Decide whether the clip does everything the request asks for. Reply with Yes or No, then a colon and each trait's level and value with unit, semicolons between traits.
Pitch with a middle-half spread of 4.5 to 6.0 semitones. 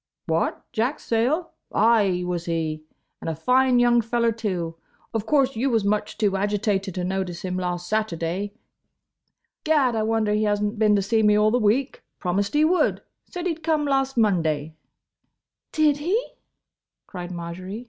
Yes: average, 5.1 semitones